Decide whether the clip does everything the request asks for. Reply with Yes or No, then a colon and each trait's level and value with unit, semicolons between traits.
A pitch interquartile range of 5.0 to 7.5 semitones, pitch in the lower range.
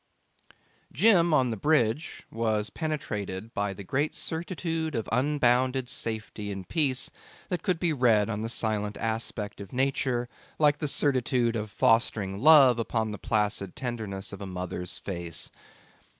Yes: wide, 5.5 semitones; low, 115 Hz